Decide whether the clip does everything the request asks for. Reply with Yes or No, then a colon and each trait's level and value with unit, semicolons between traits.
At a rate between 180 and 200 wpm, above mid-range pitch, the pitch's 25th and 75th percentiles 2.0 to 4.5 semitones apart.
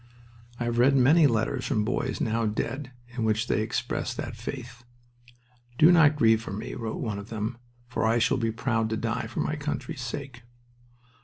No: average, 185 wpm; low, 120 Hz; average, 2.9 semitones